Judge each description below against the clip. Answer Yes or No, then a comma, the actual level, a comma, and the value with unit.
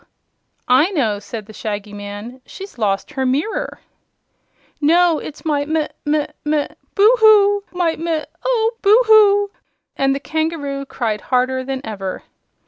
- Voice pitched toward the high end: Yes, very high, 295 Hz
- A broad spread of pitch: Yes, wide, 7.3 semitones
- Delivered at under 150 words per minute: Yes, average, 140 wpm